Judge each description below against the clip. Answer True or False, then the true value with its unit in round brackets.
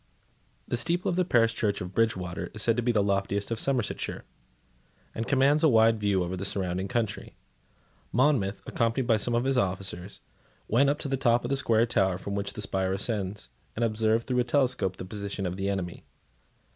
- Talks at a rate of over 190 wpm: True (200 wpm)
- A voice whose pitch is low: True (110 Hz)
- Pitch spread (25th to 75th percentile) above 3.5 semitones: True (3.9 semitones)